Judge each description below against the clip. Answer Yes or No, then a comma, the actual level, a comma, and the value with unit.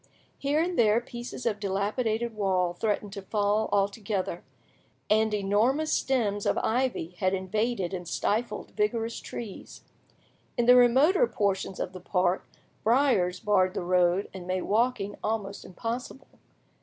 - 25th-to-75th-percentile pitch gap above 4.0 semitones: No, average, 3.7 semitones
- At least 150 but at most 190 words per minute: No, slow, 135 wpm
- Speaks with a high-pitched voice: Yes, high, 210 Hz